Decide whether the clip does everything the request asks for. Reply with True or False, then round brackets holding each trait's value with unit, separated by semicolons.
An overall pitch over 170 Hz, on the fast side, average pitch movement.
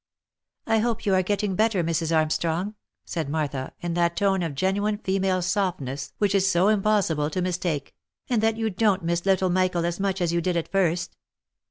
True (185 Hz; 210 wpm; 3.1 semitones)